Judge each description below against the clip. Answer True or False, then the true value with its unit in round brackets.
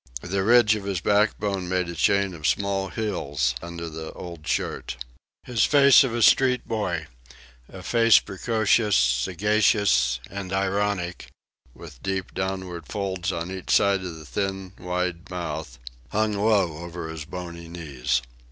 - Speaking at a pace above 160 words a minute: False (145 wpm)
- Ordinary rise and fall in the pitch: True (3.4 semitones)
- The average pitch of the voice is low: True (95 Hz)